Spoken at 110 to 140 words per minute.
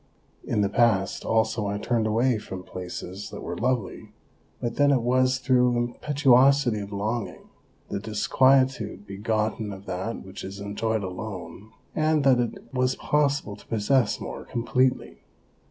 No: average, 150 wpm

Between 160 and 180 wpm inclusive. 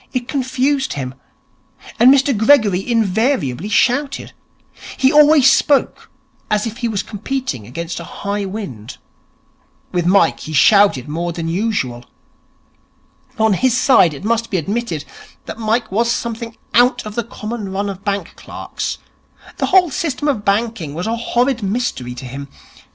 No: average, 150 wpm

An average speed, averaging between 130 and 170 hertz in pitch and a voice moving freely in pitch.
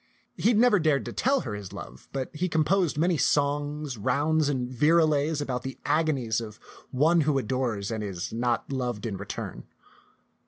No: average, 170 wpm; medium, 140 Hz; average, 4.8 semitones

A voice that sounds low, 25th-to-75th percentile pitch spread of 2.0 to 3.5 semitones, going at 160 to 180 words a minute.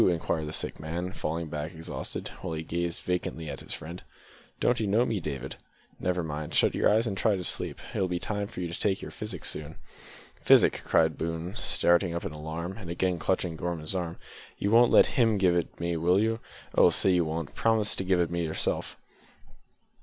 No: very low, 85 Hz; average, 2.9 semitones; fast, 205 wpm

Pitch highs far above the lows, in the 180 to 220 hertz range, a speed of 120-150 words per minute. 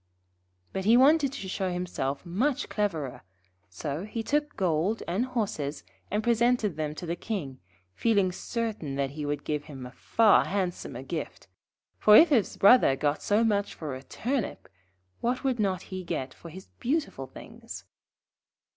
No: wide, 7.5 semitones; medium, 185 Hz; average, 165 wpm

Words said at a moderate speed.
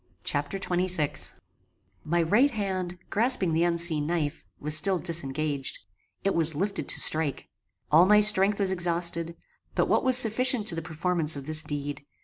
Yes: average, 155 wpm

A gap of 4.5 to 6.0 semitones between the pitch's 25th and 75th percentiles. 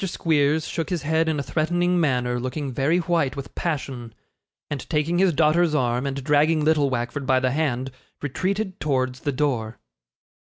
No: average, 3.8 semitones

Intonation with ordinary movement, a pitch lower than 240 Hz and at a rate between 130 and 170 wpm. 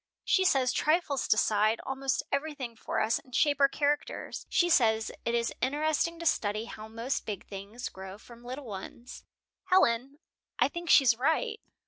No: average, 4.8 semitones; very high, 255 Hz; average, 160 wpm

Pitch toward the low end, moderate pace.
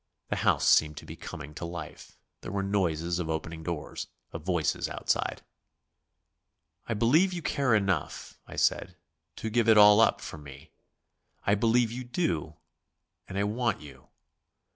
Yes: low, 100 Hz; average, 160 wpm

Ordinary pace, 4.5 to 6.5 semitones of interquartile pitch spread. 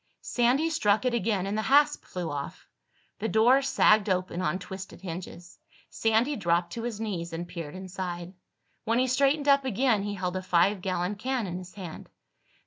Yes: average, 180 wpm; average, 5.0 semitones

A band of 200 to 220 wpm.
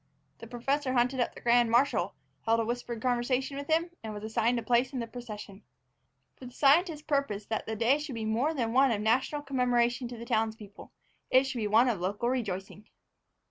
Yes: fast, 205 wpm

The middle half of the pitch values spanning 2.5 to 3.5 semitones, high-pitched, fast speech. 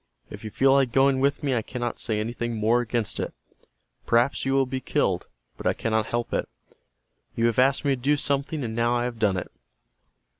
No: average, 2.8 semitones; low, 120 Hz; fast, 215 wpm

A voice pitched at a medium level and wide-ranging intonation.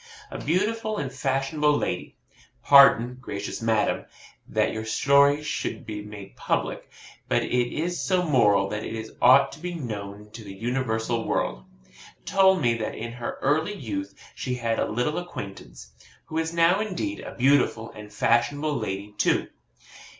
No: low, 125 Hz; wide, 5.7 semitones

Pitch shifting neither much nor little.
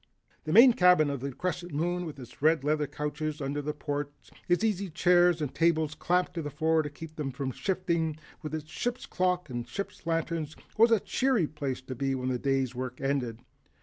Yes: average, 4.0 semitones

